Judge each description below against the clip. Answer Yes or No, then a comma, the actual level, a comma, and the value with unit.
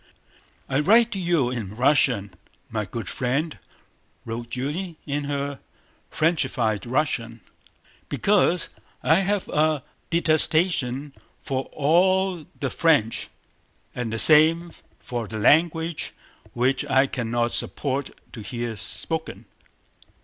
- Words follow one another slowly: Yes, slow, 105 wpm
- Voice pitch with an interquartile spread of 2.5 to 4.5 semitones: No, wide, 5.4 semitones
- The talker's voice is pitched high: No, medium, 140 Hz